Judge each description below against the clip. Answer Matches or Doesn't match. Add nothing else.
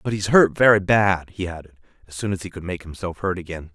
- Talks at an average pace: Doesn't match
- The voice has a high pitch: Doesn't match